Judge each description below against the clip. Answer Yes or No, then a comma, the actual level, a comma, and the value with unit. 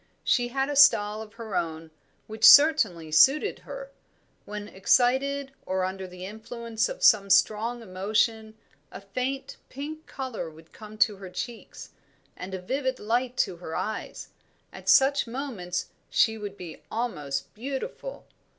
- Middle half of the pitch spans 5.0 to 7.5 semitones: Yes, wide, 5.5 semitones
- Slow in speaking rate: No, average, 145 wpm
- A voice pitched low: No, high, 220 Hz